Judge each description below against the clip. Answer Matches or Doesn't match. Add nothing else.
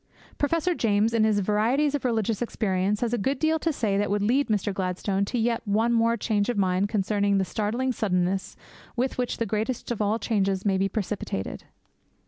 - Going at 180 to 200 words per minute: Matches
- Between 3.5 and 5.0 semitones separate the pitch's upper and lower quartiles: Doesn't match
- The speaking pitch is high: Matches